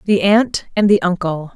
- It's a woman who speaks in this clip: Yes, female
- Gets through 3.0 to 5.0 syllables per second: Yes, 4.7 syllables/s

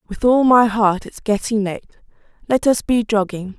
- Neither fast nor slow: Yes, average, 185 wpm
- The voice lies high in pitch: Yes, high, 220 Hz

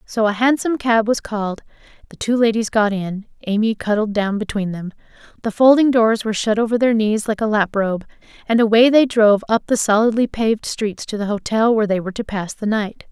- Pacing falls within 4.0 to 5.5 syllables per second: No, 5.7 syllables/s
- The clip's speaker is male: No, female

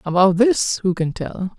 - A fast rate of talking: No, average, 190 wpm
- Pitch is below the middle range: No, high, 195 Hz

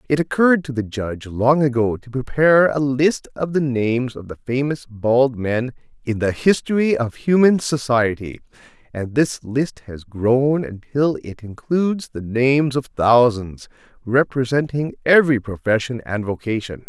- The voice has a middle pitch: No, low, 130 Hz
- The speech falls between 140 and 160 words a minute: Yes, average, 150 wpm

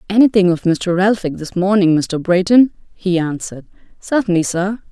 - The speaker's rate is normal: Yes, average, 145 wpm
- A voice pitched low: No, high, 190 Hz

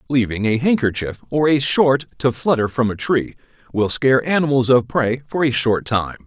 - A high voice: No, low, 125 Hz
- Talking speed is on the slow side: No, average, 190 wpm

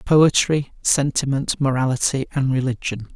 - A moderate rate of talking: No, slow, 95 wpm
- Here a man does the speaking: Yes, male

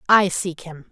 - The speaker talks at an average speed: Yes, average, 195 wpm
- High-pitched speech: No, medium, 175 Hz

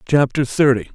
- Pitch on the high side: No, low, 135 Hz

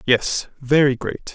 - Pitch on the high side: No, low, 135 Hz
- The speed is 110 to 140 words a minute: Yes, slow, 135 wpm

